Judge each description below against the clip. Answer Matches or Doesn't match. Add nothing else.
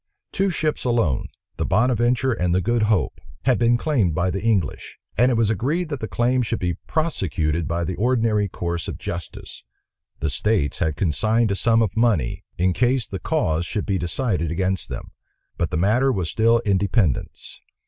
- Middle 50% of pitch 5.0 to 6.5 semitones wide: Matches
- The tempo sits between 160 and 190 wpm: Matches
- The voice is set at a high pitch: Doesn't match